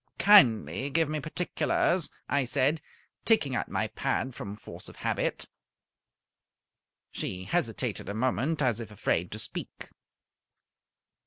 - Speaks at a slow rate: Yes, slow, 120 wpm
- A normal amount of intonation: No, wide, 5.8 semitones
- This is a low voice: Yes, low, 130 Hz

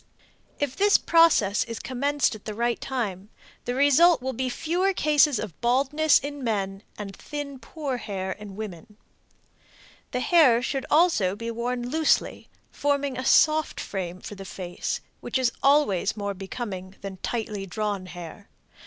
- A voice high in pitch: Yes, high, 240 Hz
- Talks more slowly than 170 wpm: Yes, average, 155 wpm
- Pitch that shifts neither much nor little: No, wide, 6.2 semitones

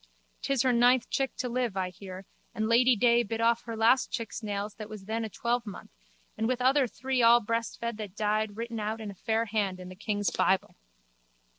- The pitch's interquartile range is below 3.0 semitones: Yes, narrow, 2.4 semitones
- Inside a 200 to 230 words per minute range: Yes, fast, 205 wpm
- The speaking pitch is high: Yes, high, 225 Hz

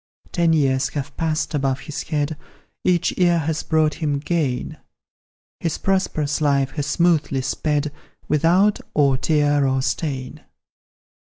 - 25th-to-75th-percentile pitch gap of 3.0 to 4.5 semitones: No, narrow, 2.6 semitones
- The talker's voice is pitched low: No, medium, 150 Hz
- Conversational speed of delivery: No, slow, 130 wpm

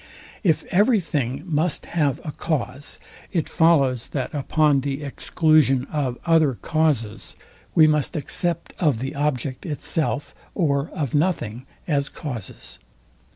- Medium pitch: Yes, medium, 145 Hz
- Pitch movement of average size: Yes, average, 3.2 semitones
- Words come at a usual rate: No, slow, 125 wpm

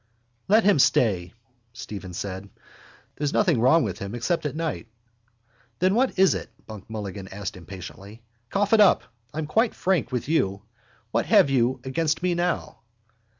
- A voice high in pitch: No, low, 130 Hz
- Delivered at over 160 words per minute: No, average, 155 wpm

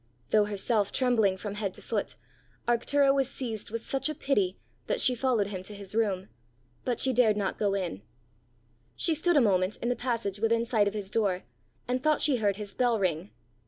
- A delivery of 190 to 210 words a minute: Yes, average, 200 wpm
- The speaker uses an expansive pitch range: No, average, 3.9 semitones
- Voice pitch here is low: No, high, 220 Hz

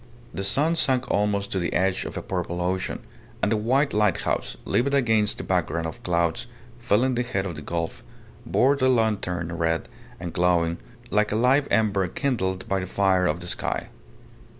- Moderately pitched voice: No, low, 100 Hz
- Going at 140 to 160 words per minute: No, average, 180 wpm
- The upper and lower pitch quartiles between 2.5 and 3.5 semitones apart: No, average, 5.1 semitones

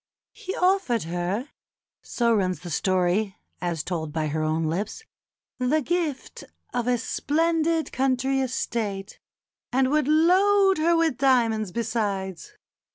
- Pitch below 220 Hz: No, high, 240 Hz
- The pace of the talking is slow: Yes, slow, 125 wpm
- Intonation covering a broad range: Yes, wide, 8.6 semitones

